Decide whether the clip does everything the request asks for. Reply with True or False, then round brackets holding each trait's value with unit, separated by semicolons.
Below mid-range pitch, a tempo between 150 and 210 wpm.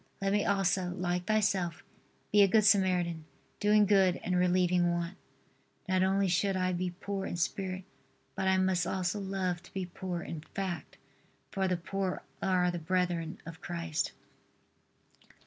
False (185 Hz; 155 wpm)